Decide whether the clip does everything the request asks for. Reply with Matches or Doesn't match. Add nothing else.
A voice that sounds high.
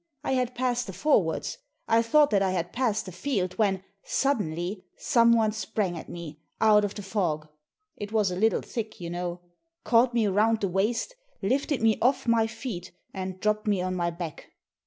Matches